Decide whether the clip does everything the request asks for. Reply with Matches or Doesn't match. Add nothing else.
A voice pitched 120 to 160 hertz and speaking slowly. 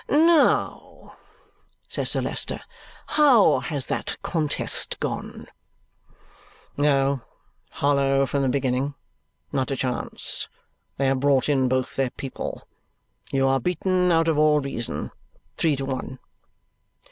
Matches